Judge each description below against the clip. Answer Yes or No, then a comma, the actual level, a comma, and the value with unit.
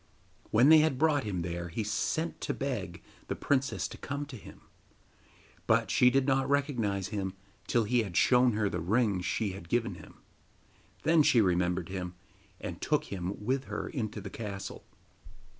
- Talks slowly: No, average, 175 wpm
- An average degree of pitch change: No, wide, 5.8 semitones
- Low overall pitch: Yes, low, 110 Hz